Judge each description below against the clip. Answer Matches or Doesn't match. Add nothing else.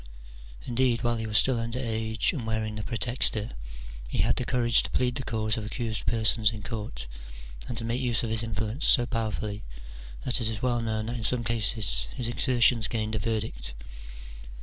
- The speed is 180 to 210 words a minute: Matches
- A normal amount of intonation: Doesn't match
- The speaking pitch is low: Matches